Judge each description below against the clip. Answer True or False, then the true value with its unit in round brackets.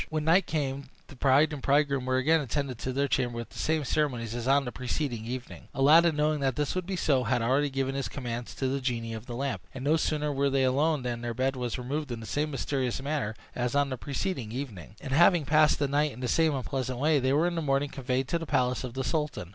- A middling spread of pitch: True (3.0 semitones)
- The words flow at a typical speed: False (255 wpm)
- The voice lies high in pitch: False (135 Hz)